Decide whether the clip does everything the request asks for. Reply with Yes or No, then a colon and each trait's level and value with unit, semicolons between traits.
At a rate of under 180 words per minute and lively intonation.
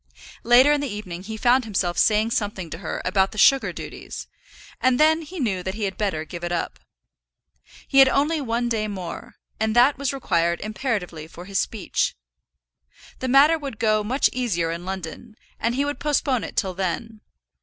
No: average, 185 wpm; wide, 5.7 semitones